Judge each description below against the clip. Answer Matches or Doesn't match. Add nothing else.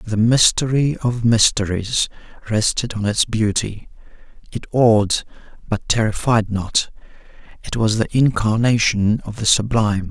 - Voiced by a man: Matches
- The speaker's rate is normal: Doesn't match